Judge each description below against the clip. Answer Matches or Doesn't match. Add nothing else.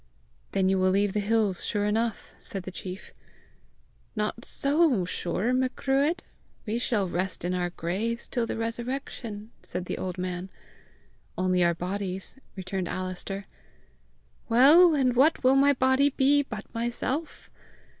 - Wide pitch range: Matches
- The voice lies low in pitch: Doesn't match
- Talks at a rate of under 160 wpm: Matches